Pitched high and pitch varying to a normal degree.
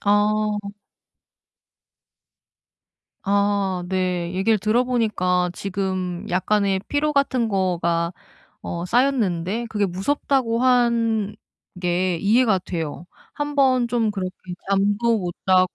Yes: high, 200 Hz; average, 4.2 semitones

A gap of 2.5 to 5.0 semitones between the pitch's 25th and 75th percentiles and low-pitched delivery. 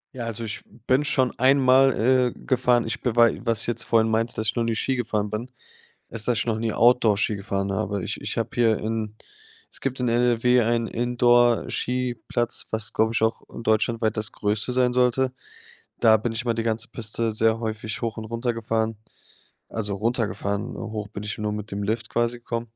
No: narrow, 1.8 semitones; low, 115 Hz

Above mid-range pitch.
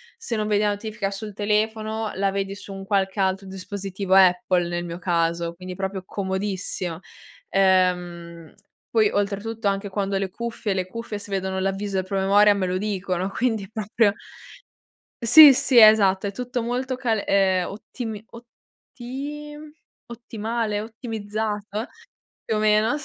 Yes: high, 200 Hz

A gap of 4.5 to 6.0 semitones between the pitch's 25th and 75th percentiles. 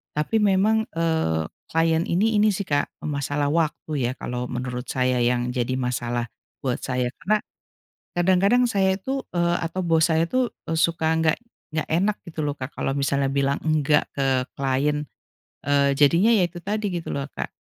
Yes: average, 5.1 semitones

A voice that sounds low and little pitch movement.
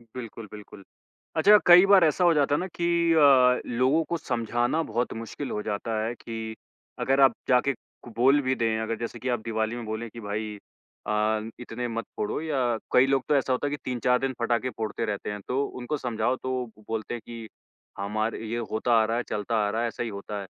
No: low, 120 Hz; average, 3.2 semitones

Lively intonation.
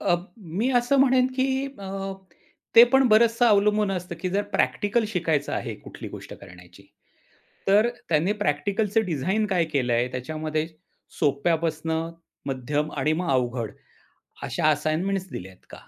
Yes: wide, 6.1 semitones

